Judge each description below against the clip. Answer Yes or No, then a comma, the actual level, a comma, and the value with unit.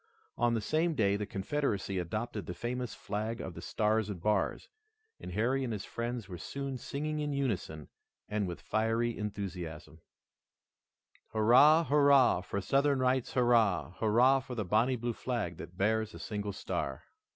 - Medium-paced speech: Yes, average, 160 wpm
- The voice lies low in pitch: Yes, low, 110 Hz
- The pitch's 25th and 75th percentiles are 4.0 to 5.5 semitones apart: Yes, average, 4.4 semitones